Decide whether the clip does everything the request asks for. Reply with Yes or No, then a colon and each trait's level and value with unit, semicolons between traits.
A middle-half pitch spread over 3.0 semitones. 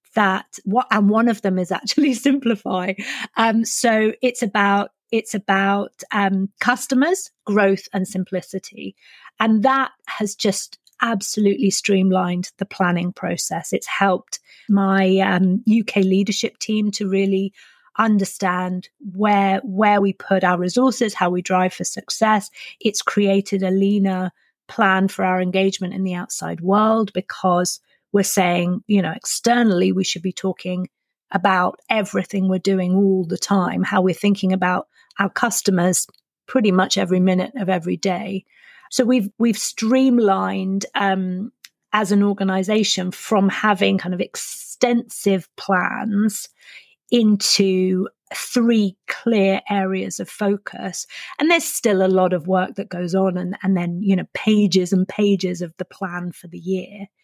No: narrow, 2.5 semitones